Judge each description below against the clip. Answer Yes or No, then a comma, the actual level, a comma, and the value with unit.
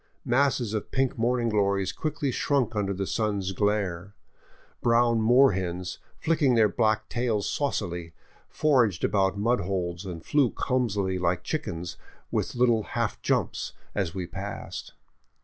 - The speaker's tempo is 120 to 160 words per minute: Yes, slow, 135 wpm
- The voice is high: No, low, 105 Hz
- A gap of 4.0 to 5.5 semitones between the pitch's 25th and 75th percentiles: Yes, average, 4.5 semitones